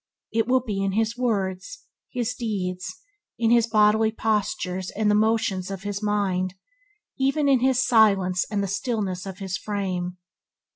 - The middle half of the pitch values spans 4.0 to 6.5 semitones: No, average, 3.2 semitones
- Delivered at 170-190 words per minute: No, average, 155 wpm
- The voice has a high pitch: Yes, high, 210 Hz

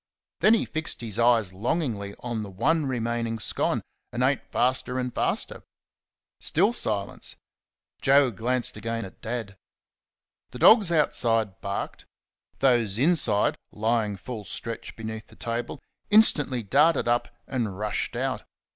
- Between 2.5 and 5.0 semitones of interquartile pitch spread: Yes, average, 3.6 semitones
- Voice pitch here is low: Yes, low, 120 Hz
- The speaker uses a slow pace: Yes, slow, 130 wpm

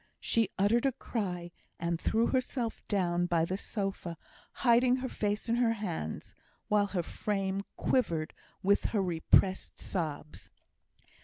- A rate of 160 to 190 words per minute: No, slow, 135 wpm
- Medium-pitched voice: No, high, 200 Hz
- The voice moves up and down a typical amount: Yes, average, 4.8 semitones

